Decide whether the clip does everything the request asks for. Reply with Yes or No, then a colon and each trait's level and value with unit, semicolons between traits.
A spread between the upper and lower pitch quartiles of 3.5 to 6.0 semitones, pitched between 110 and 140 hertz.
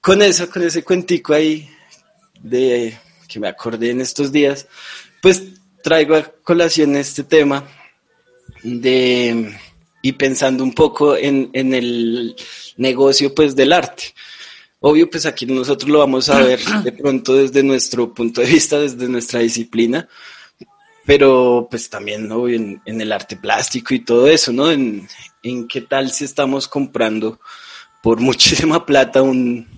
Yes: average, 4.1 semitones; low, 135 Hz